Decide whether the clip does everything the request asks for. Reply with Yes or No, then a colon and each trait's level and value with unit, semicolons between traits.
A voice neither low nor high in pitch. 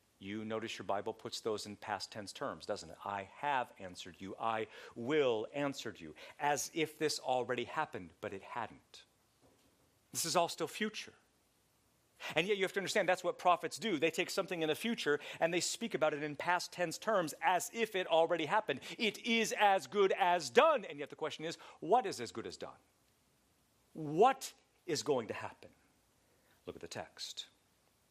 Yes: medium, 160 Hz